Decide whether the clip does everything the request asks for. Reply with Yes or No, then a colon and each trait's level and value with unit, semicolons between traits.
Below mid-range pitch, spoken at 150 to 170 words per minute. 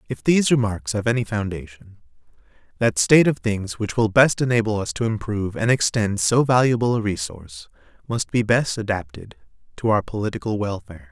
Yes: low, 105 Hz; average, 165 wpm